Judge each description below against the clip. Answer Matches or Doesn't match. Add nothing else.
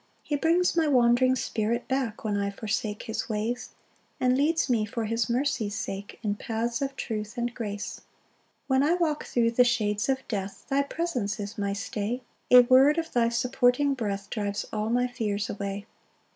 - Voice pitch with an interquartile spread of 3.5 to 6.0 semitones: Matches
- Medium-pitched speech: Doesn't match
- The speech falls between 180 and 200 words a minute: Matches